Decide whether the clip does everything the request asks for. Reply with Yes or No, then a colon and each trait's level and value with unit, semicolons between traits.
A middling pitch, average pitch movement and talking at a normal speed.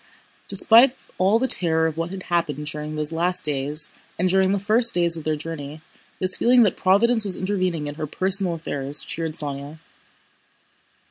Yes: medium, 170 Hz; average, 4.1 semitones; average, 175 wpm